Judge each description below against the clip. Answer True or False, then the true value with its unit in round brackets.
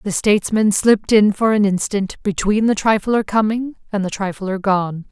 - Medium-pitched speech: False (205 Hz)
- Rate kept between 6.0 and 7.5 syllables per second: False (4.8 syllables/s)